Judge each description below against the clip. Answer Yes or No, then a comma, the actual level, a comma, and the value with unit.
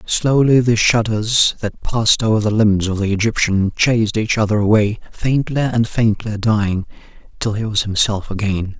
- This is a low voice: Yes, low, 110 Hz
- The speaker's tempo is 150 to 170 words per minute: Yes, average, 165 wpm